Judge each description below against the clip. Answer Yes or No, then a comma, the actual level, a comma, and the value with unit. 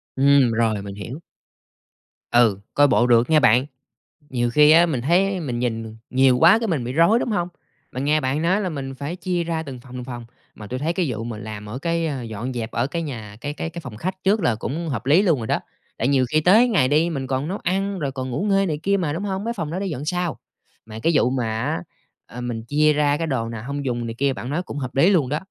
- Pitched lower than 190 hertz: Yes, medium, 140 Hz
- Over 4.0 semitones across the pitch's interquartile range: Yes, wide, 5.6 semitones